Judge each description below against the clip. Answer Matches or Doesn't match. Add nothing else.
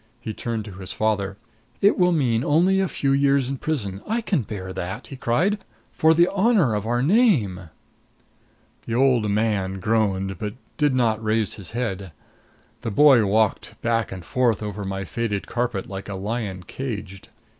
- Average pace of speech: Matches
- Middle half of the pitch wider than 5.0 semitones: Matches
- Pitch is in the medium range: Doesn't match